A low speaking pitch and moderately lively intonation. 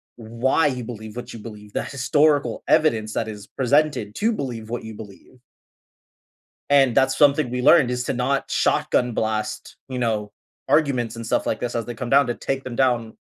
Yes: low, 125 Hz; average, 3.5 semitones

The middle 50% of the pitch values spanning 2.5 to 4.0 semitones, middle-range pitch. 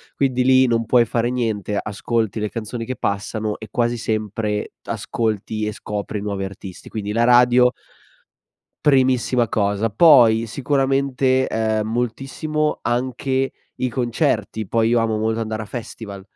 No: average, 2.8 semitones; low, 115 Hz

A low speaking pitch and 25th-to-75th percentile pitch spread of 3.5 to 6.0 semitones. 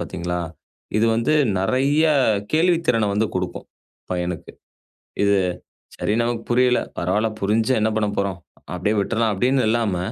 Yes: low, 110 Hz; average, 4.1 semitones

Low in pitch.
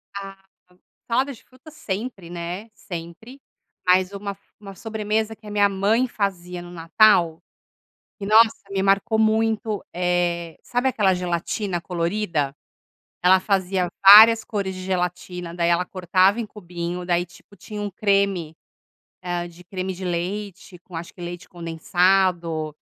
No: high, 190 Hz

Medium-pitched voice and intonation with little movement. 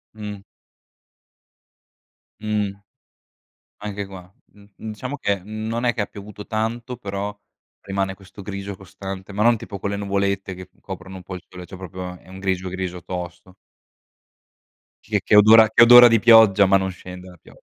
No: low, 100 Hz; narrow, 2.2 semitones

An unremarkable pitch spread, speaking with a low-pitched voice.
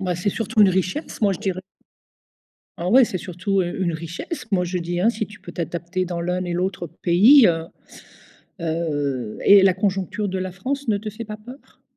No: average, 3.2 semitones; medium, 185 Hz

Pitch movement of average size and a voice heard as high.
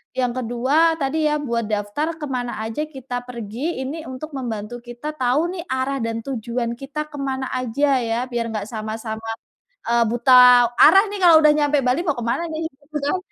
Yes: average, 4.1 semitones; very high, 255 Hz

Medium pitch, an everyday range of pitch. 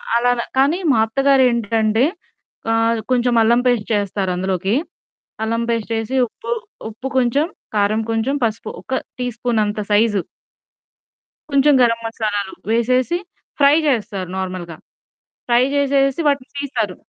No: high, 230 Hz; average, 3.3 semitones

